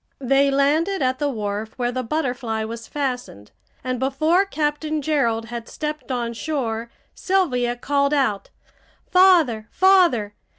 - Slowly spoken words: Yes, slow, 130 wpm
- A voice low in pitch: No, very high, 265 Hz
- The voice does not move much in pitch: No, average, 4.6 semitones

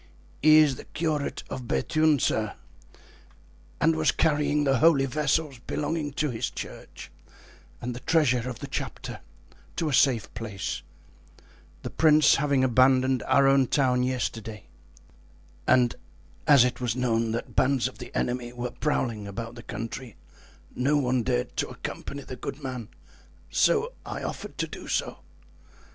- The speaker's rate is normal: Yes, average, 145 wpm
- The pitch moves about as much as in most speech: Yes, average, 3.7 semitones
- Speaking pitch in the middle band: No, low, 130 Hz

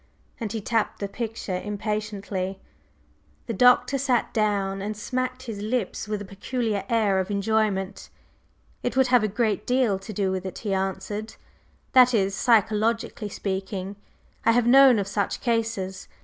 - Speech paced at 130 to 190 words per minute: Yes, average, 155 wpm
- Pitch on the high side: Yes, high, 210 Hz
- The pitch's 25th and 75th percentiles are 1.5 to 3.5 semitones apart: Yes, average, 3.0 semitones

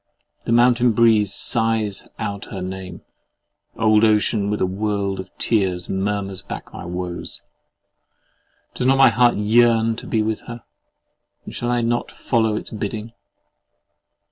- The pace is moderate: Yes, average, 145 wpm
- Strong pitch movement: No, average, 2.9 semitones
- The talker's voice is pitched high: No, low, 110 Hz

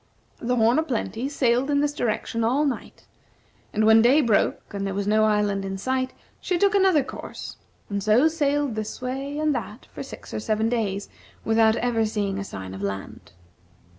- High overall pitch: Yes, high, 230 Hz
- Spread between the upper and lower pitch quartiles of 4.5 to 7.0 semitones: Yes, average, 4.8 semitones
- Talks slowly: No, average, 190 wpm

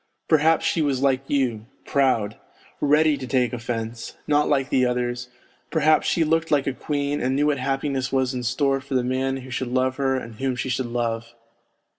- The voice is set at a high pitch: No, low, 130 Hz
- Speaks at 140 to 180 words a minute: No, average, 195 wpm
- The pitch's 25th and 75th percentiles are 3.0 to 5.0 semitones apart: No, narrow, 2.5 semitones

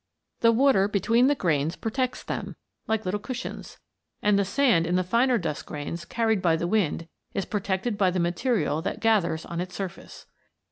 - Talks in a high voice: Yes, high, 195 Hz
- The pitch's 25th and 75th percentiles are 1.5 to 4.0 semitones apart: No, average, 5.0 semitones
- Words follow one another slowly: No, average, 180 wpm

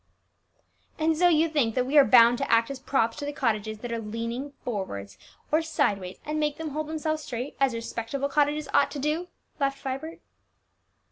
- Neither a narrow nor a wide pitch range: Yes, average, 4.8 semitones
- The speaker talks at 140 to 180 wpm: No, average, 190 wpm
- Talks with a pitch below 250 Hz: No, very high, 275 Hz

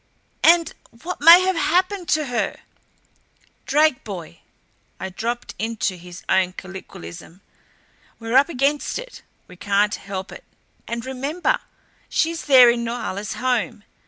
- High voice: Yes, high, 240 Hz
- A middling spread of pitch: No, wide, 7.7 semitones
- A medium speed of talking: No, slow, 130 wpm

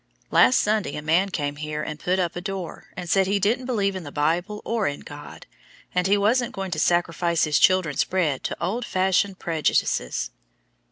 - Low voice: No, medium, 180 Hz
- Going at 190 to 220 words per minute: Yes, average, 200 wpm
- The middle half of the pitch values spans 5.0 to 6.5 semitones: No, average, 4.3 semitones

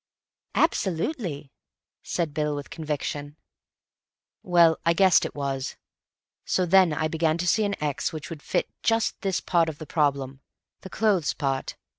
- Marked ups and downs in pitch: No, average, 3.8 semitones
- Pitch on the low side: No, medium, 160 Hz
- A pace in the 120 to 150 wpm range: Yes, average, 145 wpm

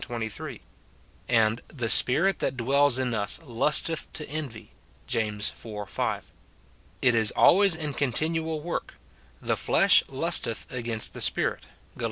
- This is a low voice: Yes, low, 125 Hz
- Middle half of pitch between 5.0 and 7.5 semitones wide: Yes, wide, 5.4 semitones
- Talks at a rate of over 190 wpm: No, average, 140 wpm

